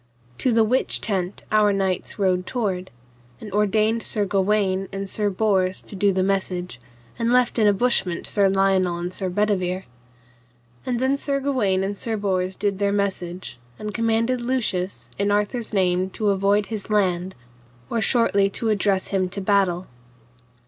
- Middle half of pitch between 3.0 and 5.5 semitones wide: No, narrow, 2.5 semitones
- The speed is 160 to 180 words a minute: Yes, average, 165 wpm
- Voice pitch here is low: No, high, 200 Hz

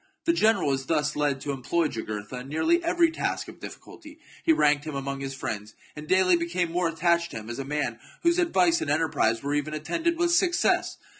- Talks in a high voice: No, medium, 155 Hz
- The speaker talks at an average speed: No, fast, 215 wpm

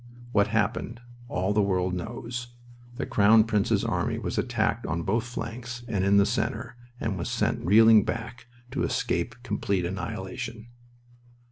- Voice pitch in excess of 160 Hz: No, low, 110 Hz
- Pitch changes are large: No, average, 3.0 semitones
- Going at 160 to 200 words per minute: No, average, 145 wpm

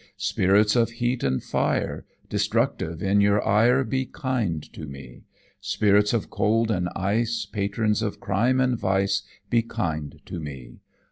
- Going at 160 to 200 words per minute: No, average, 145 wpm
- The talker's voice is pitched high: No, low, 105 Hz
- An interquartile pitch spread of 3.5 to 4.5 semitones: Yes, average, 4.0 semitones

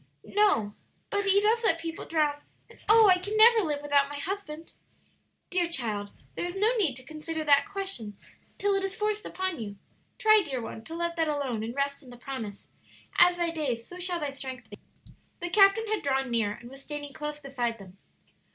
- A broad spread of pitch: Yes, wide, 6.8 semitones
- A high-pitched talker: Yes, very high, 305 Hz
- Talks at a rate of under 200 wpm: No, fast, 205 wpm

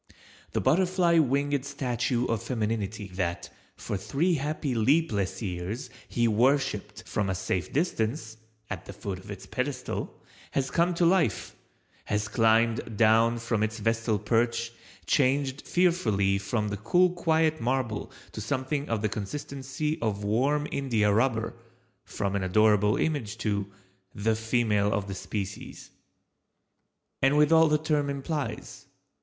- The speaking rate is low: Yes, slow, 130 wpm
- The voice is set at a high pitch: No, low, 115 Hz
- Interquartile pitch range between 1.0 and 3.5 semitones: No, average, 5.3 semitones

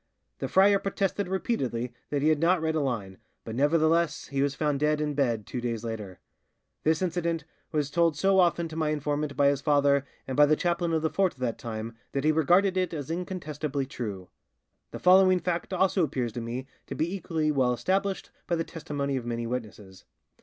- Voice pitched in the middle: Yes, medium, 150 Hz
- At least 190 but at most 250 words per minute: Yes, fast, 205 wpm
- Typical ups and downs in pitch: Yes, average, 4.8 semitones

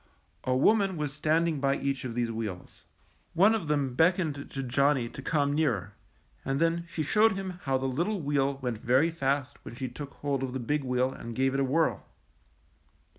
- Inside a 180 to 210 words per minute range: Yes, average, 195 wpm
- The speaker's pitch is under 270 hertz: Yes, medium, 140 Hz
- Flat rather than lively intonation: No, average, 3.8 semitones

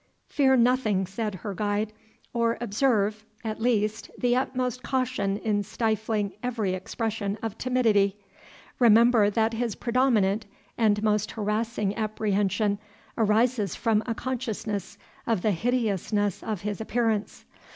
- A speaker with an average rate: No, slow, 120 wpm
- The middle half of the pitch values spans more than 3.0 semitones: No, narrow, 2.4 semitones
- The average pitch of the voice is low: No, high, 220 Hz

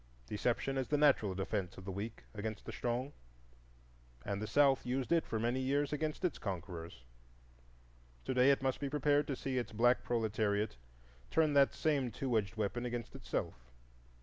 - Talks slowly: No, average, 175 wpm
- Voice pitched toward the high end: No, low, 120 Hz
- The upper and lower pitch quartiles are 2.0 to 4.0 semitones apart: No, average, 4.7 semitones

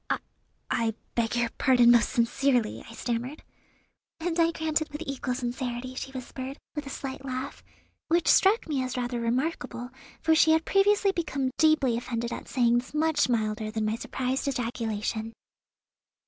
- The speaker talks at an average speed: Yes, average, 160 wpm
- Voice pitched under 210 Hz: No, very high, 255 Hz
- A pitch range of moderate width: Yes, average, 4.1 semitones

